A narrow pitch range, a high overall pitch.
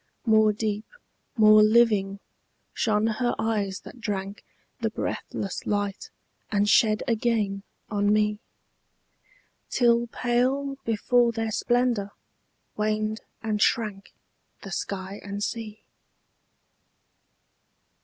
Yes: narrow, 2.1 semitones; high, 215 Hz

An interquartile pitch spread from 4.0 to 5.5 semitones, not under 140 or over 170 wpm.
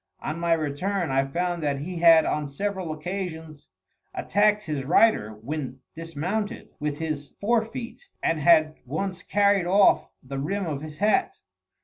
Yes: average, 5.0 semitones; average, 150 wpm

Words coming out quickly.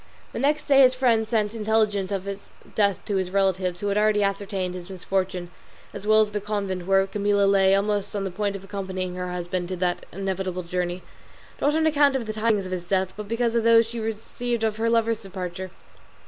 Yes: fast, 215 wpm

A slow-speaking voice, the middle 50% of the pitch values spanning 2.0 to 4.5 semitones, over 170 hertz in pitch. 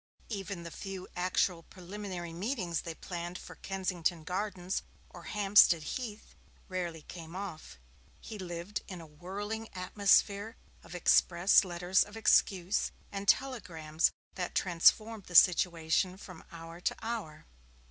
Yes: slow, 125 wpm; average, 2.9 semitones; medium, 185 Hz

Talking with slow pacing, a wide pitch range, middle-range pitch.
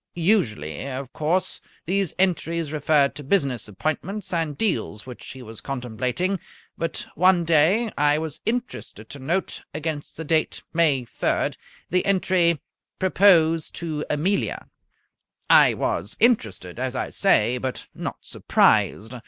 Yes: slow, 130 wpm; wide, 5.7 semitones; medium, 155 Hz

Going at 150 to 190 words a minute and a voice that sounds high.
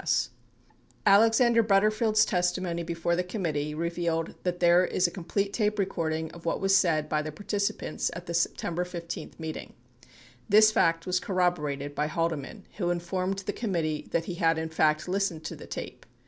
No: average, 175 wpm; medium, 175 Hz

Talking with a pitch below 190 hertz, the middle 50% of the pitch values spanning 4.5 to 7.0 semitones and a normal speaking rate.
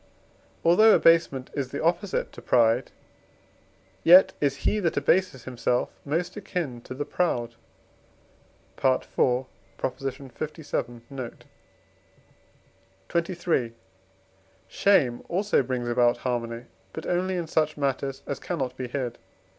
No: medium, 140 Hz; wide, 5.5 semitones; slow, 110 wpm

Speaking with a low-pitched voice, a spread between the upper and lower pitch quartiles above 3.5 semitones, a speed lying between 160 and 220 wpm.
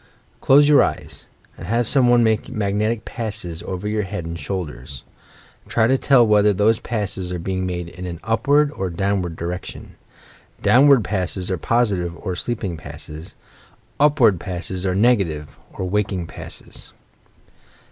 No: low, 100 Hz; average, 4.3 semitones; average, 150 wpm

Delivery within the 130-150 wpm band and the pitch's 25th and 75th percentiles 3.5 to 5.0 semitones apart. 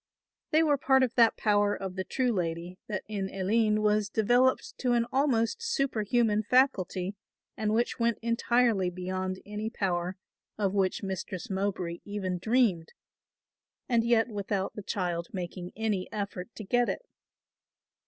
Yes: average, 145 wpm; average, 3.9 semitones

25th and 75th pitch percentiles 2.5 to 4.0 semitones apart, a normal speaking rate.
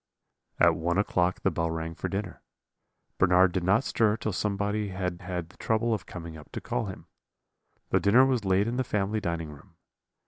Yes: average, 3.5 semitones; average, 195 wpm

